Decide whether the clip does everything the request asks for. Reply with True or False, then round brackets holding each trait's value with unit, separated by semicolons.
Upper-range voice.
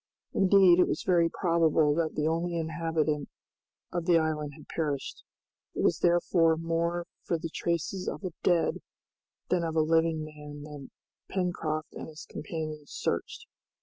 False (165 Hz)